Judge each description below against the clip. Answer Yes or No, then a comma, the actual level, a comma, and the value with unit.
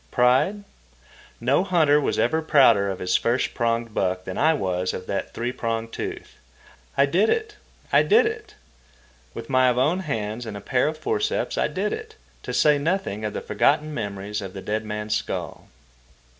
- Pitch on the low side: Yes, low, 125 Hz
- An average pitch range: No, wide, 7.0 semitones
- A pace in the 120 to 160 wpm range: No, average, 180 wpm